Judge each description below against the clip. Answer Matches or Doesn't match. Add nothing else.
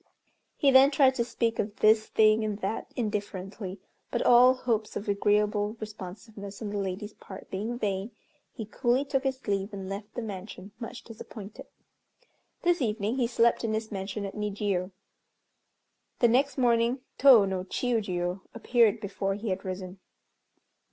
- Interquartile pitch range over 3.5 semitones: Doesn't match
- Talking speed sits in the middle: Matches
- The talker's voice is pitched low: Doesn't match